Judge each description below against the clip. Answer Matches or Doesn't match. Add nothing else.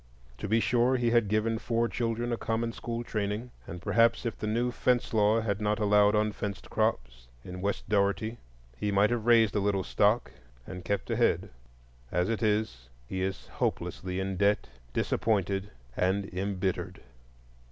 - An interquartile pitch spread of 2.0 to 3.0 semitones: Matches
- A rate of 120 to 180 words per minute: Matches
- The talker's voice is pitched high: Doesn't match